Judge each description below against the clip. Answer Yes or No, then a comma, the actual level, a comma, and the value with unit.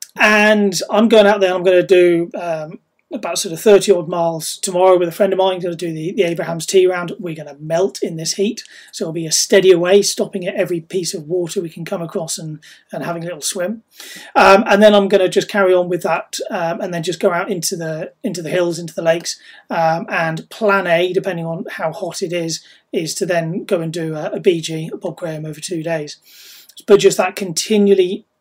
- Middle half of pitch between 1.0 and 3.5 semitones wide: Yes, average, 3.0 semitones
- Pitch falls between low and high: Yes, medium, 180 Hz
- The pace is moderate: No, fast, 245 wpm